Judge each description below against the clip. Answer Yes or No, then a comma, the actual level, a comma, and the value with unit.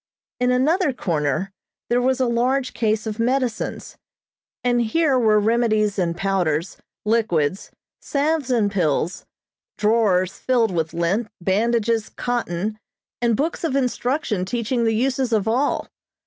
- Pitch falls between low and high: No, high, 230 Hz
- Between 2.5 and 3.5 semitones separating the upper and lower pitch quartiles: No, average, 4.2 semitones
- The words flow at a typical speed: No, slow, 130 wpm